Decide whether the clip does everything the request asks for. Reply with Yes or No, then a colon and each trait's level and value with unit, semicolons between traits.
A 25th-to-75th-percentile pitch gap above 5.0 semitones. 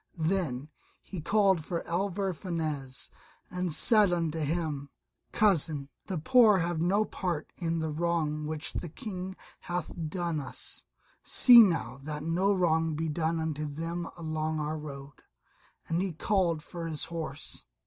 No: average, 2.9 semitones